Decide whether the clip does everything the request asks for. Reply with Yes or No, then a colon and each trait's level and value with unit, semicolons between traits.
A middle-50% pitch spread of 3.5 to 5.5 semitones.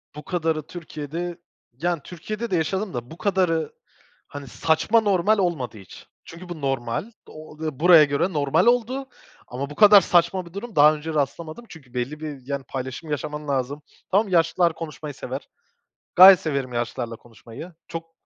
Yes: average, 4.1 semitones